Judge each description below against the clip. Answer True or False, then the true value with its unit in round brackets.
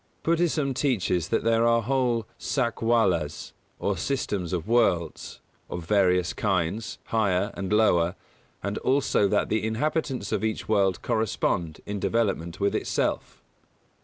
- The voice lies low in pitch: True (105 Hz)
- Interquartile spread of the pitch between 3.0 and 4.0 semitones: False (4.4 semitones)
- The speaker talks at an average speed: False (130 wpm)